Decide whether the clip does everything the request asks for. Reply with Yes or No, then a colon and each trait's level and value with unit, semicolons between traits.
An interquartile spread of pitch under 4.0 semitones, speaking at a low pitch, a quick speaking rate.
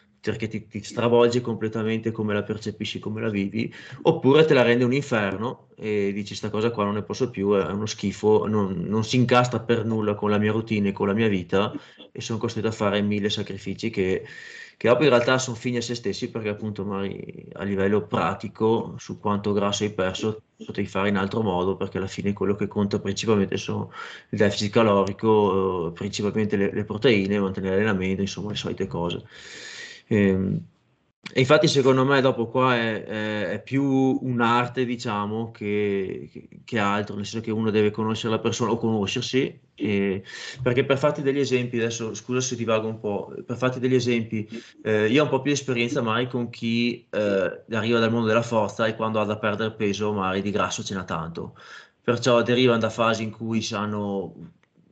Yes: narrow, 2.6 semitones; low, 110 Hz; fast, 190 wpm